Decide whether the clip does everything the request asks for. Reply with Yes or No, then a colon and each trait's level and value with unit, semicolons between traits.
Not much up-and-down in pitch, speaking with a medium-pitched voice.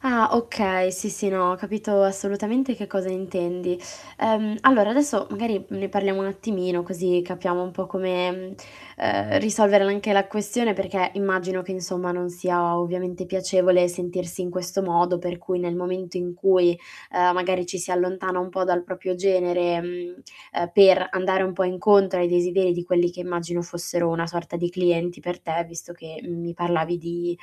Yes: narrow, 1.7 semitones; medium, 180 Hz